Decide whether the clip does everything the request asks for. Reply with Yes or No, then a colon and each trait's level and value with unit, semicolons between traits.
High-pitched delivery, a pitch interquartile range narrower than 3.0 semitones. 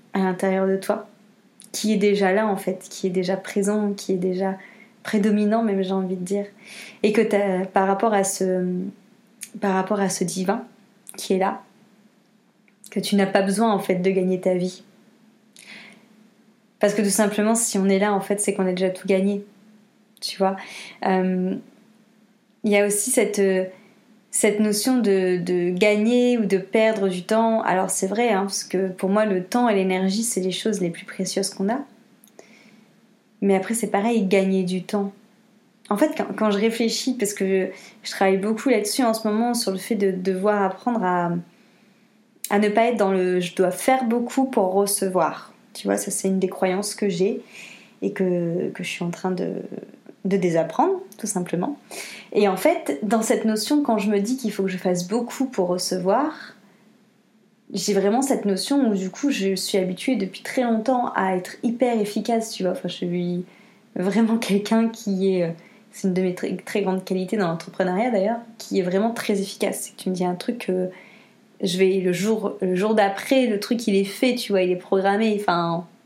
Yes: high, 205 Hz; narrow, 2.6 semitones